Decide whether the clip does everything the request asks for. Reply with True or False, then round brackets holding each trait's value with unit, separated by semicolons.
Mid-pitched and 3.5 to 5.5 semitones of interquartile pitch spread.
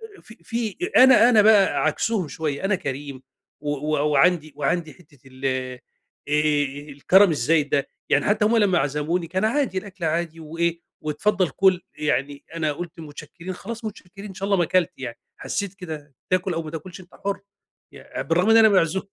True (170 Hz; 4.7 semitones)